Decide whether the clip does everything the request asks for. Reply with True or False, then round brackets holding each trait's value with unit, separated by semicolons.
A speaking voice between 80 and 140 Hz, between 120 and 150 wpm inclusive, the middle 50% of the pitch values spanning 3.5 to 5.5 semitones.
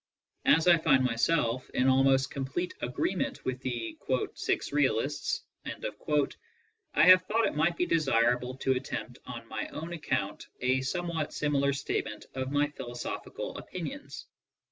True (135 Hz; 140 wpm; 3.8 semitones)